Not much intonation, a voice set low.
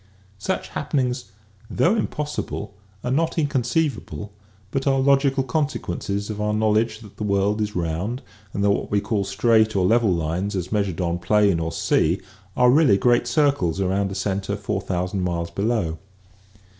No: average, 4.5 semitones; low, 105 Hz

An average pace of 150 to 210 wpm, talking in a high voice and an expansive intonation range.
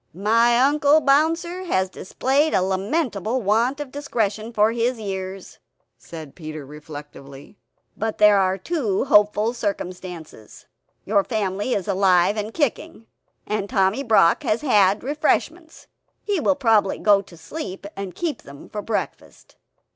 No: slow, 135 wpm; high, 210 Hz; wide, 5.8 semitones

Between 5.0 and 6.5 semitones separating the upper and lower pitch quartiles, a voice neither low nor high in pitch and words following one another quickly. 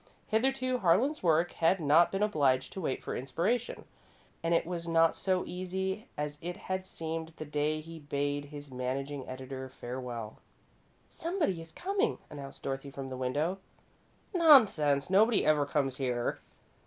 No: wide, 5.4 semitones; medium, 160 Hz; average, 150 wpm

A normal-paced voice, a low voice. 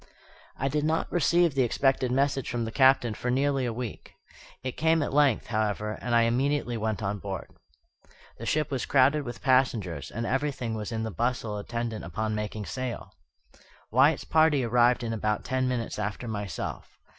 Yes: average, 175 wpm; low, 120 Hz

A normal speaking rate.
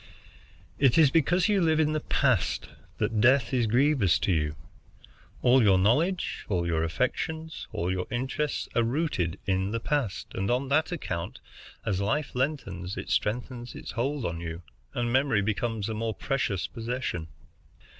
Yes: average, 160 wpm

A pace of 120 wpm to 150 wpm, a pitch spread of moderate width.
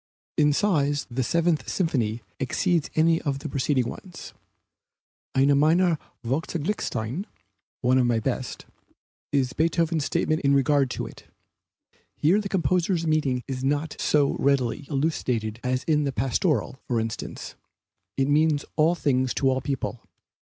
Yes: average, 140 wpm; average, 3.7 semitones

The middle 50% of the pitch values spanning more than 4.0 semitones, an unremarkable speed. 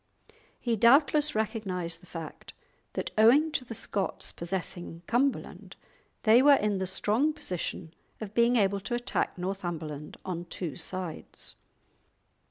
No: average, 5.3 semitones; slow, 130 wpm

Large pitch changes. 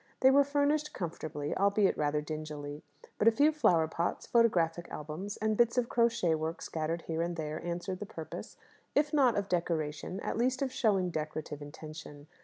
Yes: wide, 6.9 semitones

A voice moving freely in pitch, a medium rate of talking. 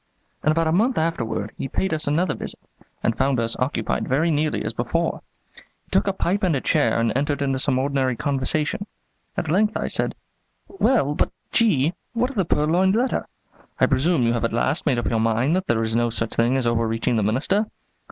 No: wide, 6.4 semitones; fast, 210 wpm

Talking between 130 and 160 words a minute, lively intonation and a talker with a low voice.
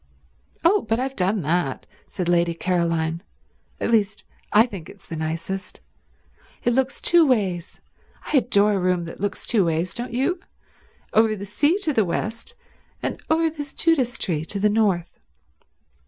No: average, 155 wpm; wide, 6.3 semitones; high, 205 Hz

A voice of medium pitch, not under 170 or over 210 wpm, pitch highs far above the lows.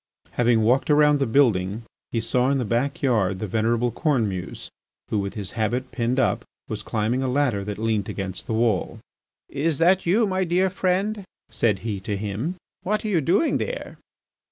No: low, 120 Hz; average, 180 wpm; wide, 6.0 semitones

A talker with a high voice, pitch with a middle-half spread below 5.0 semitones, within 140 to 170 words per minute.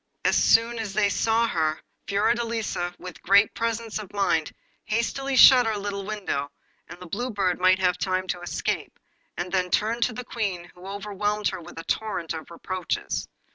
No: high, 200 Hz; average, 3.7 semitones; average, 180 wpm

